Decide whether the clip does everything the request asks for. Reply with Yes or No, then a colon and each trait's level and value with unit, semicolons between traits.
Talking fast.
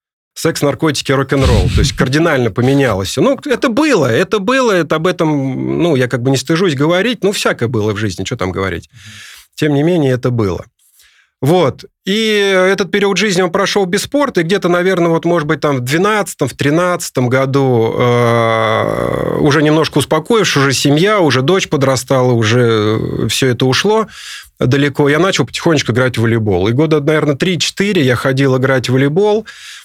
Yes: fast, 170 wpm